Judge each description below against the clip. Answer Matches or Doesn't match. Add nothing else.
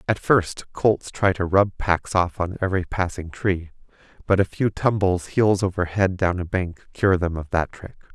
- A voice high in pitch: Doesn't match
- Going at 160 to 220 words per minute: Matches